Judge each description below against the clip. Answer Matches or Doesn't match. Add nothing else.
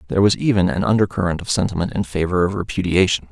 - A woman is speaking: Doesn't match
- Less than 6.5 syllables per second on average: Doesn't match